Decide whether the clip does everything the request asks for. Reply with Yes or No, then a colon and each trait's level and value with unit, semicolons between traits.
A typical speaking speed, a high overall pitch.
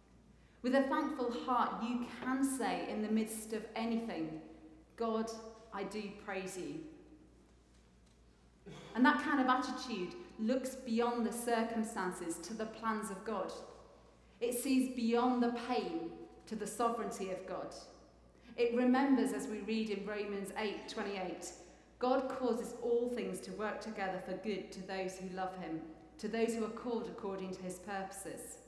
Yes: average, 155 wpm; high, 225 Hz